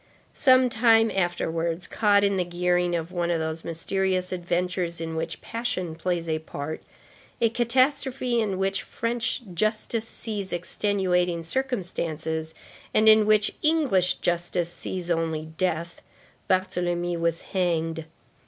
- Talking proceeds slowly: Yes, slow, 125 wpm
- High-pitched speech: No, medium, 180 Hz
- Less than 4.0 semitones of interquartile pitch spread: No, average, 4.3 semitones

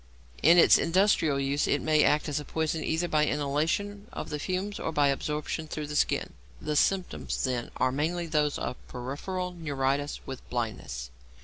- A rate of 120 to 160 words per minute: No, average, 175 wpm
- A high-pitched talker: No, medium, 150 Hz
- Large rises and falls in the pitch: No, average, 3.2 semitones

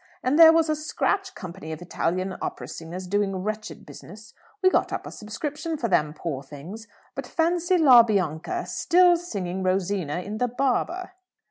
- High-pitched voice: Yes, high, 215 Hz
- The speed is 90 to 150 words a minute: No, average, 165 wpm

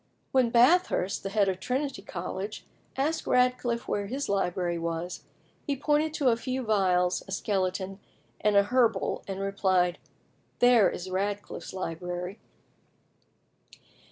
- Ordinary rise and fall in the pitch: Yes, average, 5.0 semitones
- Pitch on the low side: No, high, 200 Hz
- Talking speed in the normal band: No, slow, 130 wpm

